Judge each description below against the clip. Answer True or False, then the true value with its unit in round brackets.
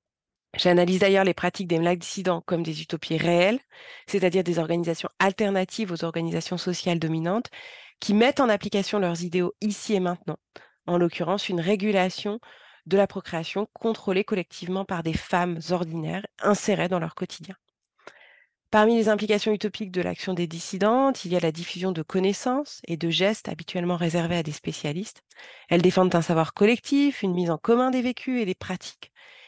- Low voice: False (185 Hz)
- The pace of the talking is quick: False (165 wpm)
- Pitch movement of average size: True (3.3 semitones)